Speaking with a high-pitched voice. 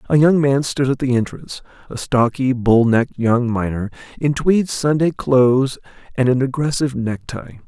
No: low, 130 Hz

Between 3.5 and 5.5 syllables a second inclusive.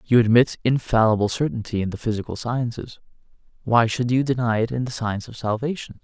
No: 5.9 syllables/s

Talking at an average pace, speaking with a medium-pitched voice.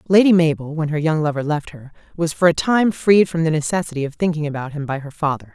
No: fast, 250 wpm; medium, 160 Hz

